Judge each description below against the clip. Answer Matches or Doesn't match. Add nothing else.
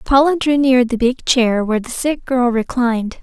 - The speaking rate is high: Matches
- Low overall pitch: Doesn't match